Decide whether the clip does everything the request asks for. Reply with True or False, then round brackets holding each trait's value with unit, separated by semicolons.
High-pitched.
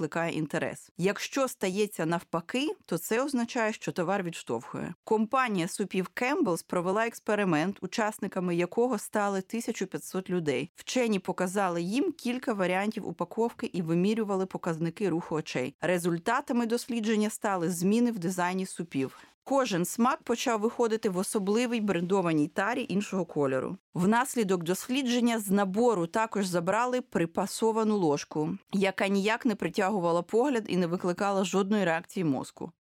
True (195 Hz)